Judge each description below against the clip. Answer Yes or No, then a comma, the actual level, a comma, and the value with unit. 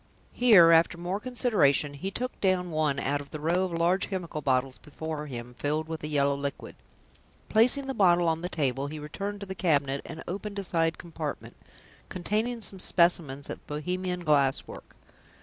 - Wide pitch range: No, average, 4.5 semitones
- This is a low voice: No, medium, 165 Hz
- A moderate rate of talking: Yes, average, 180 wpm